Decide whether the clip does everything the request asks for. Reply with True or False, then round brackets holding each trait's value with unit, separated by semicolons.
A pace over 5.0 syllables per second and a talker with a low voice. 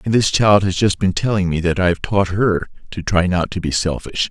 True (5.2 syllables/s; 95 Hz)